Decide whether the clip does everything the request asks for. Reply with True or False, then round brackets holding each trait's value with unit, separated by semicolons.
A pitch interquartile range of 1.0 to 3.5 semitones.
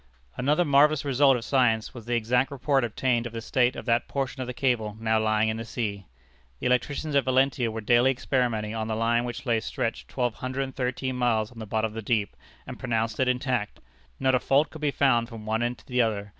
True (2.8 semitones)